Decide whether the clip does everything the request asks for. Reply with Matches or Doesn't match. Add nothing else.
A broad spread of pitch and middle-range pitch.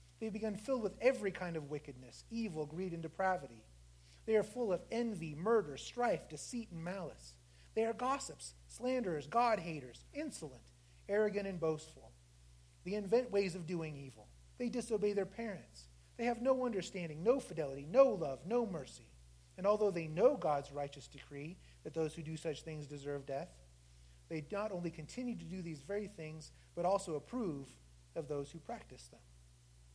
Matches